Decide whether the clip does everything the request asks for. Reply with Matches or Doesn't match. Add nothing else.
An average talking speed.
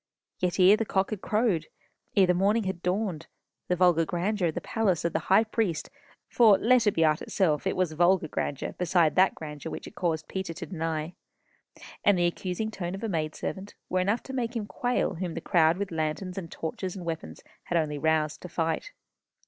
Doesn't match